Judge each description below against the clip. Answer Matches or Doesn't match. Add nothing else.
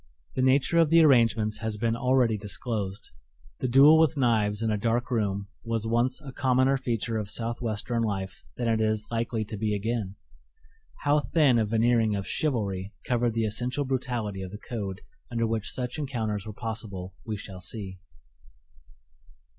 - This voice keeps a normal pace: Matches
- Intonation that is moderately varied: Matches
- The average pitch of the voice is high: Doesn't match